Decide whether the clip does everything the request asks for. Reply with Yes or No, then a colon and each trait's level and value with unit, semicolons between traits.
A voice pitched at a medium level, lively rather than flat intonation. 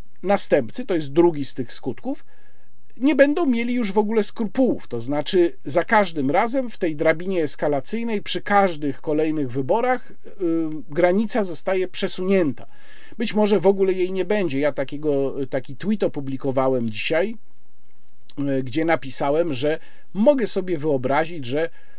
Yes: medium, 175 Hz; wide, 6.5 semitones